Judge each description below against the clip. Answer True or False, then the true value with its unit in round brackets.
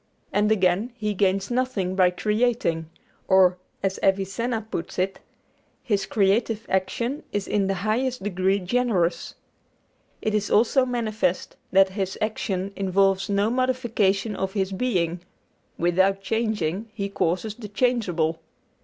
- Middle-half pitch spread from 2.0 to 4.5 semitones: True (2.9 semitones)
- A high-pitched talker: True (200 Hz)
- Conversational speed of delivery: False (125 wpm)